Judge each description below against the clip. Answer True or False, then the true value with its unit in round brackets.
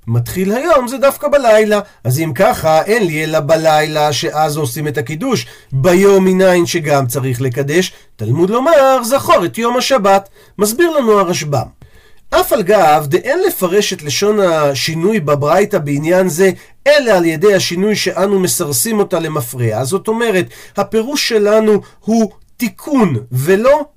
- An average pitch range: False (6.0 semitones)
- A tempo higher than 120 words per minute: True (145 wpm)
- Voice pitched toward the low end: False (185 Hz)